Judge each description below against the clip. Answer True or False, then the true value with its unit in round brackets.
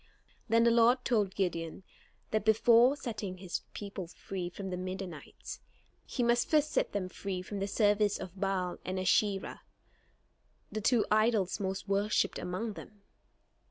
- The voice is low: False (200 Hz)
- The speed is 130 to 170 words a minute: True (150 wpm)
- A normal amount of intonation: True (3.0 semitones)